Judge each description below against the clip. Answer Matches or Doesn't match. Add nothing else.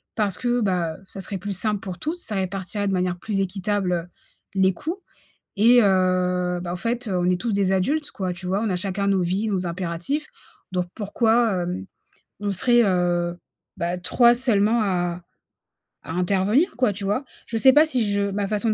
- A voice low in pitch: Doesn't match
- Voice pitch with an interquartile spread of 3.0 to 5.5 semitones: Matches